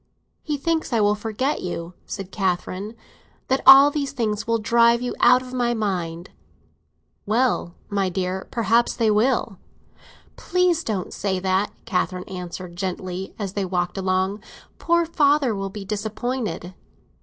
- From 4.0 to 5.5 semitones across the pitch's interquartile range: Yes, average, 4.8 semitones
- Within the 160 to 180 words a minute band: No, average, 145 wpm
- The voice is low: No, high, 210 Hz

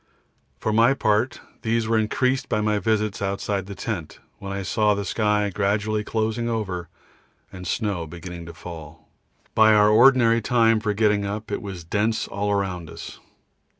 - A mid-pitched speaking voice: No, low, 105 Hz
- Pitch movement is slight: Yes, narrow, 2.3 semitones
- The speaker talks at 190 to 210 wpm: No, average, 165 wpm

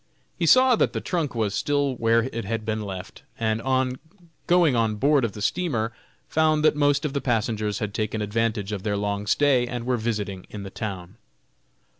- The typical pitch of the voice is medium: No, low, 115 Hz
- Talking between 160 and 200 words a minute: Yes, average, 195 wpm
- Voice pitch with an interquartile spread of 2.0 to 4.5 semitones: No, average, 4.9 semitones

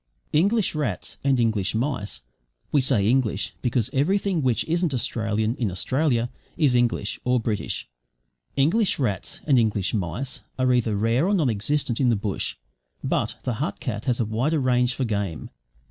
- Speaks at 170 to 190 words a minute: No, average, 160 wpm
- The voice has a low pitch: Yes, low, 125 Hz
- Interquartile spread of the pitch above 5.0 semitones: No, average, 4.3 semitones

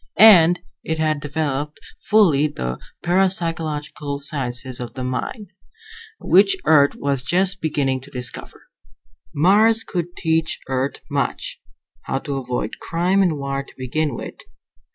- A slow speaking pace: Yes, slow, 130 wpm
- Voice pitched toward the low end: No, medium, 150 Hz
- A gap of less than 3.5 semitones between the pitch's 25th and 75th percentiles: No, average, 4.4 semitones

